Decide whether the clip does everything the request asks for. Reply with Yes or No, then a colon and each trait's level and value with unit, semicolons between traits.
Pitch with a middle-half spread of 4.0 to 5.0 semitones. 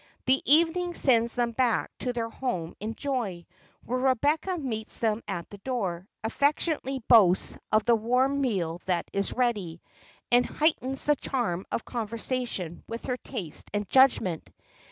Yes: average, 4.6 semitones